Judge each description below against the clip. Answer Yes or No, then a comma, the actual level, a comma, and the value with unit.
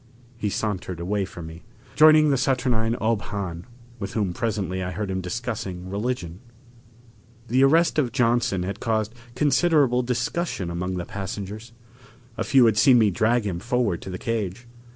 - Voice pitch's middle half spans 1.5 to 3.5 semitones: No, average, 4.8 semitones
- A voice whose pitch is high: No, low, 110 Hz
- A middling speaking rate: Yes, average, 160 wpm